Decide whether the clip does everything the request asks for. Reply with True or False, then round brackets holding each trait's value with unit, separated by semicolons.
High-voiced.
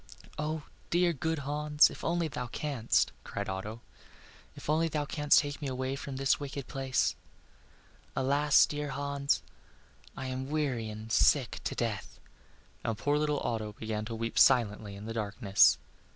False (135 Hz)